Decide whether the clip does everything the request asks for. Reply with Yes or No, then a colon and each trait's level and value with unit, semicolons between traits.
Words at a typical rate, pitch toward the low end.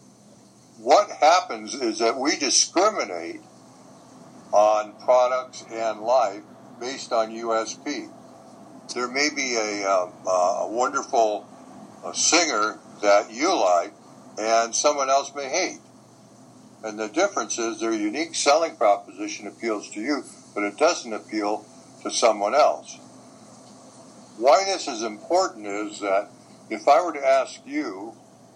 No: slow, 125 wpm; low, 125 Hz